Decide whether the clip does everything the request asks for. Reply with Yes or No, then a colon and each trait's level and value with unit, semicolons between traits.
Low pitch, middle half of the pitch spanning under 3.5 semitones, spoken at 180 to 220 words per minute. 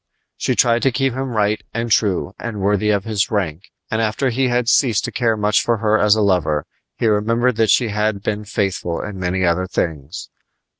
Yes: low, 105 Hz; average, 3.0 semitones; fast, 205 wpm